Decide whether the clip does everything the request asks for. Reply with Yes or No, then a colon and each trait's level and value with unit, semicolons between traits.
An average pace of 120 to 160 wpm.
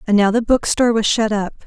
No: fast, 250 wpm